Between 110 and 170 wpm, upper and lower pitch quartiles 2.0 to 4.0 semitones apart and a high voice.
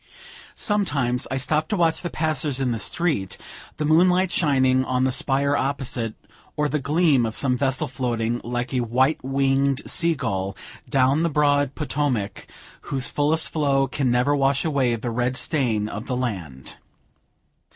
No: average, 160 wpm; average, 3.3 semitones; low, 135 Hz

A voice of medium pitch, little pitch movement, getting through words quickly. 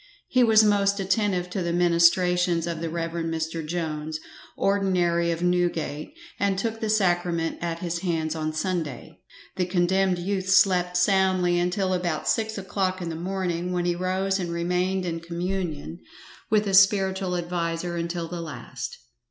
No: medium, 180 Hz; narrow, 2.1 semitones; average, 155 wpm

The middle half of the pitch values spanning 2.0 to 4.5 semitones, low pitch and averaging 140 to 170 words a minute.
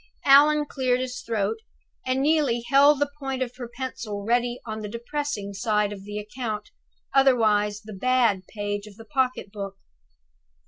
No: average, 3.9 semitones; high, 235 Hz; average, 155 wpm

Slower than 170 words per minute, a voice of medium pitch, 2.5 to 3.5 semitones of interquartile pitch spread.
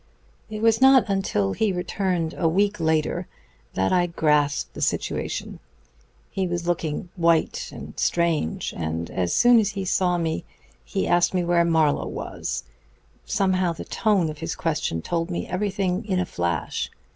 Yes: average, 160 wpm; medium, 175 Hz; average, 3.2 semitones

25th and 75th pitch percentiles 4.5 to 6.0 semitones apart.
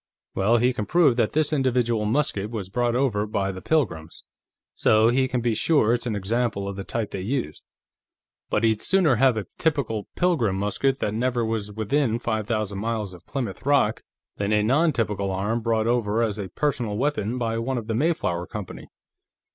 No: average, 3.7 semitones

